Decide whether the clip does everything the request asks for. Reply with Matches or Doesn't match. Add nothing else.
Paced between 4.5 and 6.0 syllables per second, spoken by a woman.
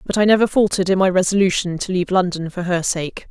Doesn't match